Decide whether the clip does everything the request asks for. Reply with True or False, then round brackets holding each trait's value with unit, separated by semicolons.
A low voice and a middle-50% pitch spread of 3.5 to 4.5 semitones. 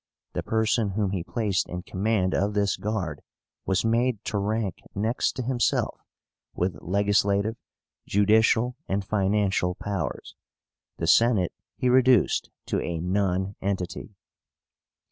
False (100 Hz; 2.8 semitones)